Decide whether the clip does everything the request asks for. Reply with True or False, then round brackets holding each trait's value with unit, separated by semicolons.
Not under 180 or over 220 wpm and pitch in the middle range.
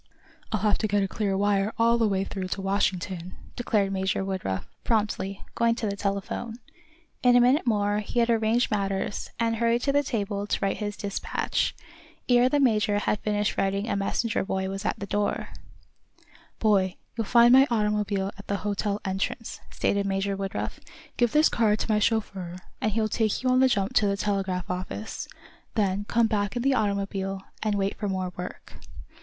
False (185 wpm; 205 Hz)